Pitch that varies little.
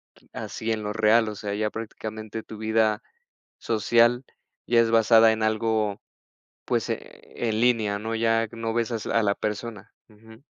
Yes: narrow, 1.1 semitones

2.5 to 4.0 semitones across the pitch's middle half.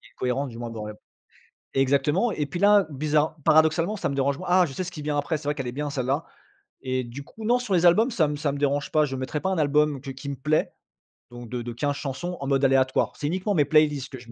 Yes: average, 3.0 semitones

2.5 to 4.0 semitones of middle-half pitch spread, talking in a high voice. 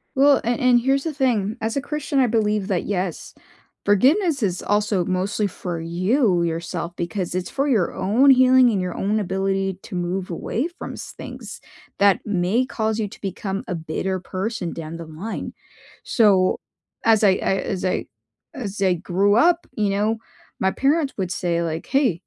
No: average, 4.8 semitones; high, 200 Hz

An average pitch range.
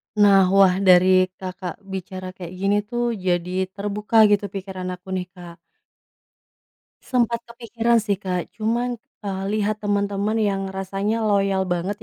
No: narrow, 2.1 semitones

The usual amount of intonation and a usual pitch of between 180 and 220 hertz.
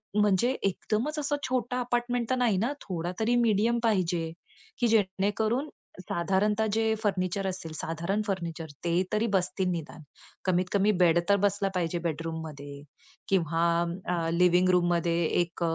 Yes: average, 4.4 semitones; high, 190 Hz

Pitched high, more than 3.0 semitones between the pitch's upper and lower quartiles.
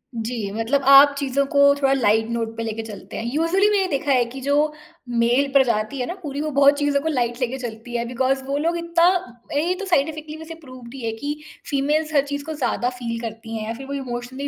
Yes: very high, 270 Hz; average, 3.7 semitones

